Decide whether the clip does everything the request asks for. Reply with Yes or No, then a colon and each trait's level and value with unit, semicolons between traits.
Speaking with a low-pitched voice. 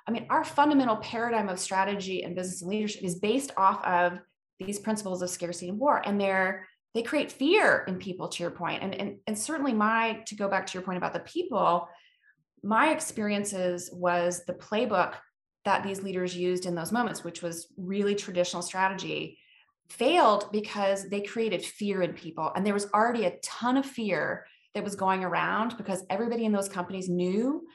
No: high, 195 Hz